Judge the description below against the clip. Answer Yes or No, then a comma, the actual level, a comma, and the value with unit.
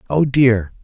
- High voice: No, low, 125 Hz